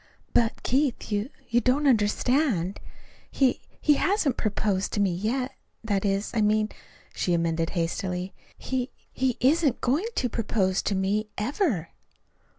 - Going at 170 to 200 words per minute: No, average, 140 wpm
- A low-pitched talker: No, high, 215 Hz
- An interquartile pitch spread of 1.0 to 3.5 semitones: No, average, 5.0 semitones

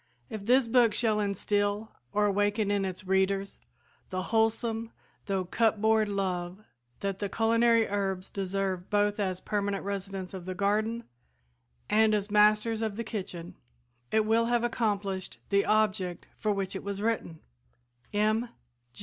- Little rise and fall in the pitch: Yes, narrow, 2.2 semitones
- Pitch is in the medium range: No, high, 205 Hz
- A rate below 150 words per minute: Yes, average, 140 wpm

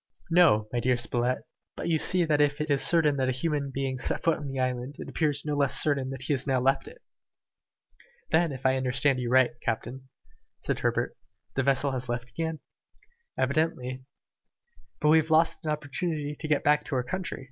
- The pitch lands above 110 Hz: Yes, medium, 140 Hz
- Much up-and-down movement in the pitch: No, average, 3.0 semitones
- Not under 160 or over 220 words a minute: Yes, average, 200 wpm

